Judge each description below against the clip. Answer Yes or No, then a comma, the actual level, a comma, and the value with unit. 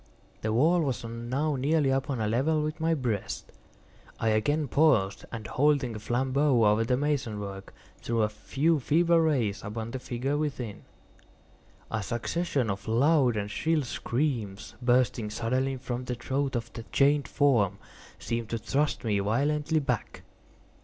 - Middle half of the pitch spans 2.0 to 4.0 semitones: No, average, 4.5 semitones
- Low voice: Yes, low, 125 Hz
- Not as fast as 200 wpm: Yes, average, 155 wpm